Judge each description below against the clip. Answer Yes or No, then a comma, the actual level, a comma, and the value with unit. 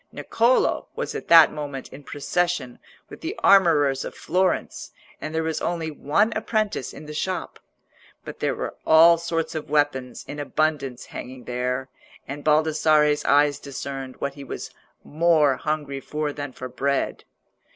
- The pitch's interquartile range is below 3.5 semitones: Yes, average, 2.9 semitones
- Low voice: No, medium, 150 Hz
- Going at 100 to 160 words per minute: Yes, average, 150 wpm